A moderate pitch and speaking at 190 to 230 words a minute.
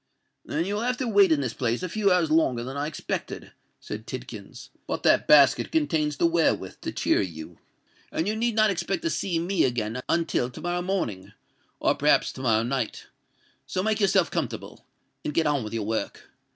Yes: medium, 155 Hz; average, 195 wpm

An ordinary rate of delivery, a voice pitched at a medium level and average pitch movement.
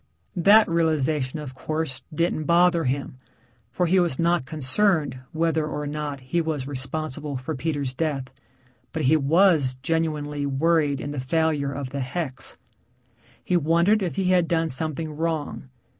Yes: average, 150 wpm; medium, 155 Hz; average, 3.2 semitones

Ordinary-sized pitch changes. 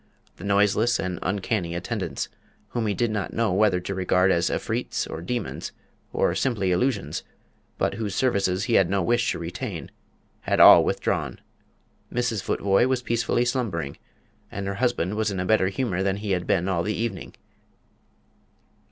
Yes: average, 3.9 semitones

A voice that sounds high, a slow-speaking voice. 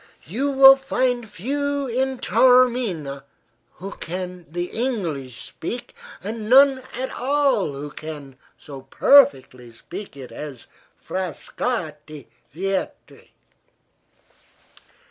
Yes: high, 195 Hz; slow, 95 wpm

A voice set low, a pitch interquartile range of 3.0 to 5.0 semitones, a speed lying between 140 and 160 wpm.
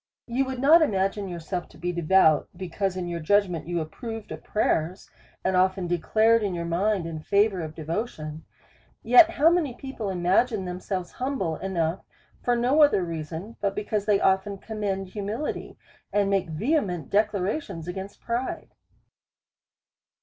No: high, 195 Hz; average, 4.3 semitones; average, 150 wpm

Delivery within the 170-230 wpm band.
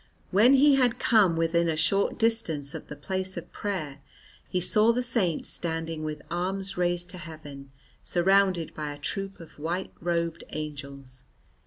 No: average, 160 wpm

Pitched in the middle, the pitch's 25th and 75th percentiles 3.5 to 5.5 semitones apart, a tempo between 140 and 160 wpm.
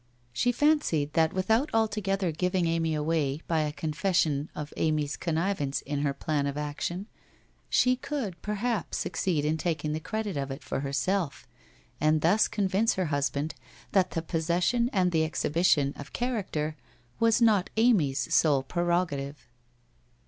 Yes: medium, 165 Hz; average, 4.8 semitones; average, 150 wpm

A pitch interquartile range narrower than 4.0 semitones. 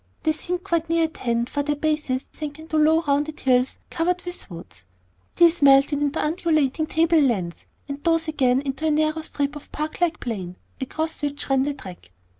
Yes: average, 3.0 semitones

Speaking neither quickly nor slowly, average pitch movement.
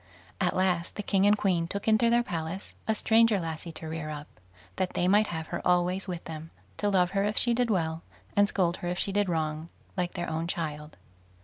No: fast, 220 wpm; average, 3.8 semitones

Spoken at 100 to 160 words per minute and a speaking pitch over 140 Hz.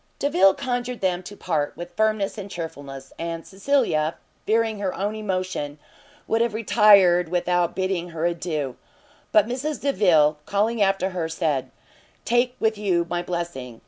Yes: average, 145 wpm; medium, 185 Hz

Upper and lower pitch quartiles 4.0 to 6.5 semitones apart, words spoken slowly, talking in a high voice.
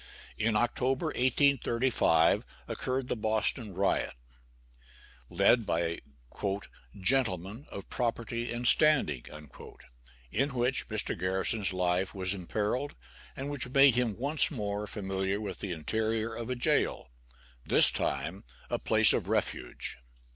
No: average, 4.8 semitones; slow, 120 wpm; low, 110 Hz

